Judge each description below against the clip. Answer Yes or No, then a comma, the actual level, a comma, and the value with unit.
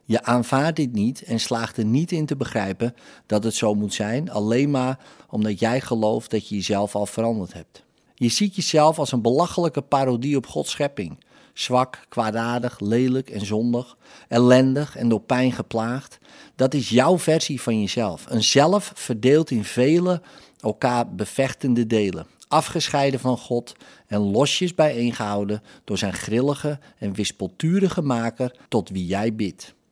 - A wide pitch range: No, average, 4.3 semitones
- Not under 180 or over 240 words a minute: No, average, 155 wpm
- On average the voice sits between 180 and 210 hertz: No, low, 120 Hz